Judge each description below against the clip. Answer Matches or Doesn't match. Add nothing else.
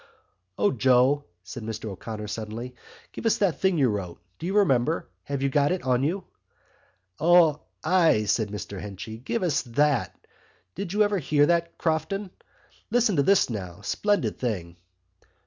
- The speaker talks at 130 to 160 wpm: Matches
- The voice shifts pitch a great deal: Matches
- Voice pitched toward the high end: Doesn't match